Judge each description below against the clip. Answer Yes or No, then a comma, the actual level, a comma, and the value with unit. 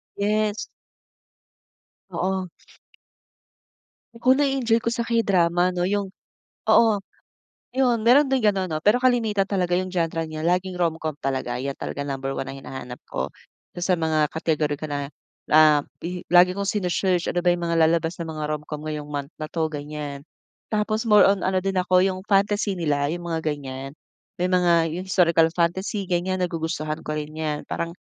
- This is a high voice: No, medium, 175 Hz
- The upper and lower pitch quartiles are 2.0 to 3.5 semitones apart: No, average, 4.1 semitones